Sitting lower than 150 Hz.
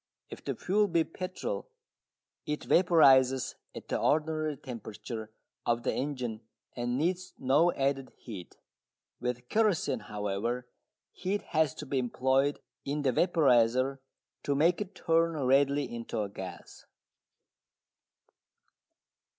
Yes: low, 135 Hz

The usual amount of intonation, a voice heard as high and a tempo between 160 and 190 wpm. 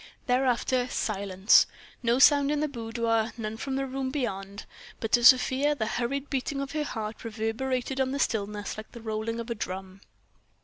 Yes: average, 3.6 semitones; high, 235 Hz; average, 175 wpm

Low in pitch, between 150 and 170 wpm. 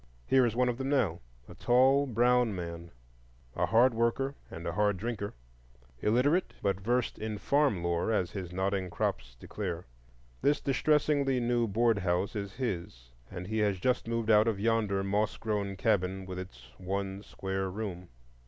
Yes: low, 105 Hz; average, 160 wpm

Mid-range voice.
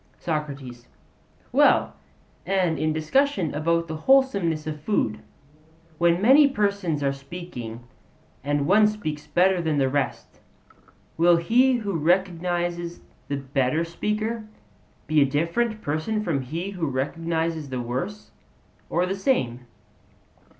Yes: medium, 170 Hz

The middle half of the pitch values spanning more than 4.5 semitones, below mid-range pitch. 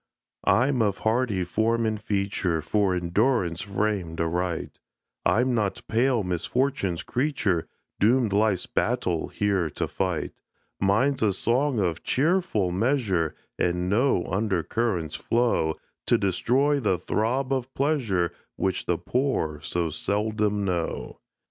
Yes: wide, 5.5 semitones; low, 105 Hz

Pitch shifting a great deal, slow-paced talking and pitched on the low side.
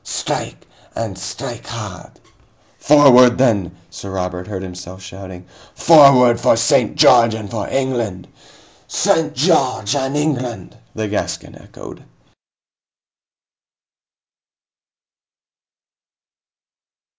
Yes: wide, 5.9 semitones; slow, 85 wpm; low, 115 Hz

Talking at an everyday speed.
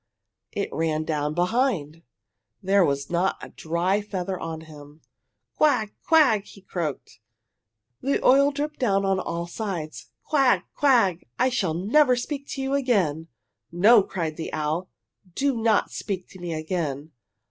Yes: average, 145 wpm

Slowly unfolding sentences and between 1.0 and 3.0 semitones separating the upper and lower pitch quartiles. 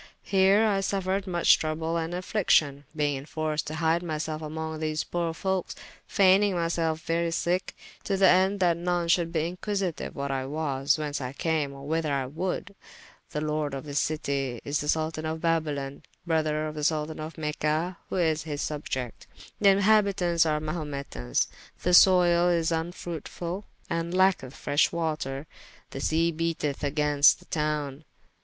No: average, 160 wpm; average, 2.7 semitones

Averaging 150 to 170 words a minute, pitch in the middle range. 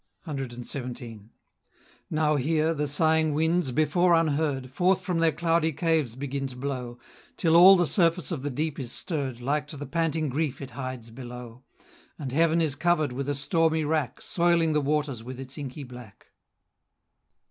Yes: average, 165 wpm; medium, 145 Hz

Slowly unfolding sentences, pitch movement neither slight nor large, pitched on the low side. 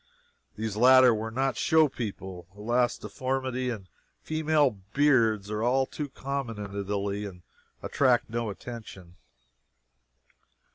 Yes: slow, 105 wpm; average, 4.2 semitones; low, 120 Hz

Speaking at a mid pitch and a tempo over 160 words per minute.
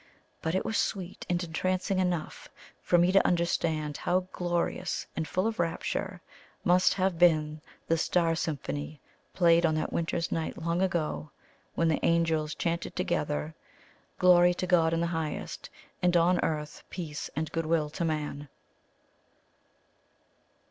No: medium, 170 Hz; average, 145 wpm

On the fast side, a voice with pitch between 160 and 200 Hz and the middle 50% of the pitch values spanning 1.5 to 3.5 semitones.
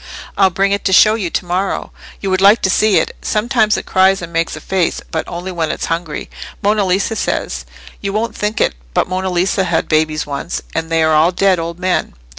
Yes: fast, 225 wpm; medium, 185 Hz; average, 3.1 semitones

